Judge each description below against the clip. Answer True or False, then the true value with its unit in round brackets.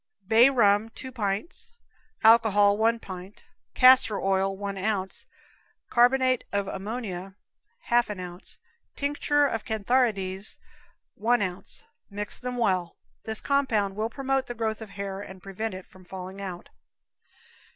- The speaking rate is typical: False (130 wpm)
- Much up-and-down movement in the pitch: False (3.7 semitones)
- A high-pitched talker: True (210 Hz)